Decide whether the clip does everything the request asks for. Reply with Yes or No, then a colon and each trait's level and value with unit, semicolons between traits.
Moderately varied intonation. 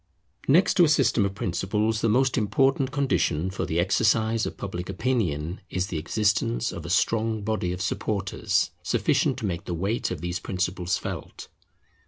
Yes: average, 4.0 semitones